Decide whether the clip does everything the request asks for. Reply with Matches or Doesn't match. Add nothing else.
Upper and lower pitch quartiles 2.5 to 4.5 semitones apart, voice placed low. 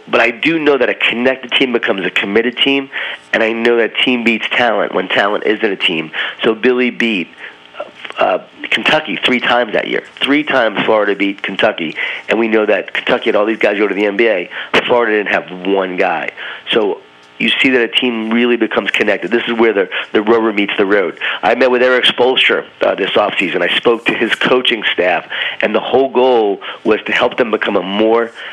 Matches